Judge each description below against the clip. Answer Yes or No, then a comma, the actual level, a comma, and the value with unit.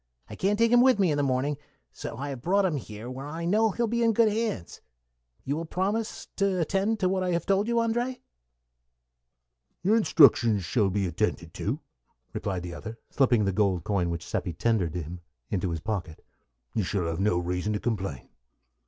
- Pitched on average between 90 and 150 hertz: Yes, low, 135 Hz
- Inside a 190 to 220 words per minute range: Yes, fast, 205 wpm